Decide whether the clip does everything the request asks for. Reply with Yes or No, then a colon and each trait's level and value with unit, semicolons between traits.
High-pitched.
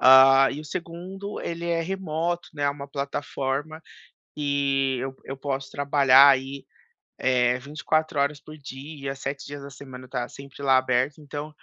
No: medium, 140 Hz